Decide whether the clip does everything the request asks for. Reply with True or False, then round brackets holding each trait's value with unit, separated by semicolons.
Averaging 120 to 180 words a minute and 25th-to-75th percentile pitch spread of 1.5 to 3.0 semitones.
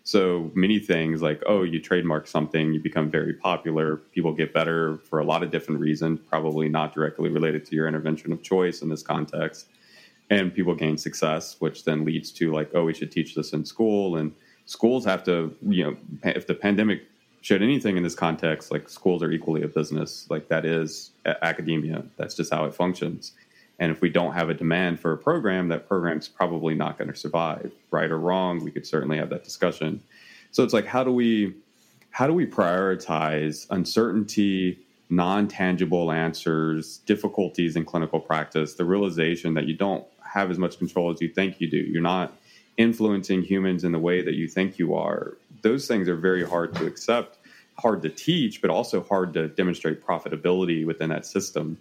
False (190 wpm; 2.7 semitones)